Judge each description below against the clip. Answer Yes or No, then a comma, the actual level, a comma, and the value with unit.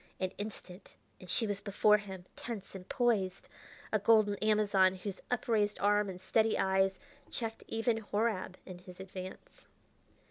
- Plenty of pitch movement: No, narrow, 2.5 semitones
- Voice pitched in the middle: No, high, 205 Hz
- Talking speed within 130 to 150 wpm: Yes, average, 145 wpm